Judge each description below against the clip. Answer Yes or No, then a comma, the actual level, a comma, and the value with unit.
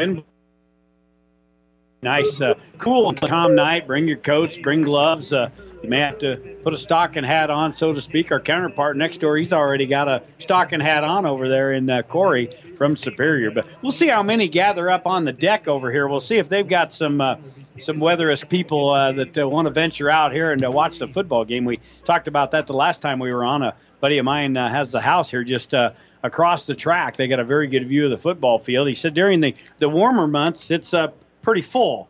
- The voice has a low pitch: No, medium, 150 Hz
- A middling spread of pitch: Yes, average, 3.9 semitones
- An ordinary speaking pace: No, fast, 230 wpm